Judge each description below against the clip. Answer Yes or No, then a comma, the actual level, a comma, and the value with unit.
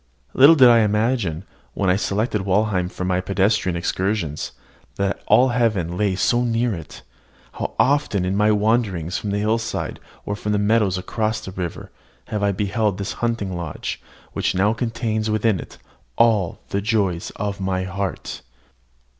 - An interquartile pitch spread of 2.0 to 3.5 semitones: Yes, average, 3.1 semitones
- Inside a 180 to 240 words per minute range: No, average, 160 wpm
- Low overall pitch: Yes, low, 105 Hz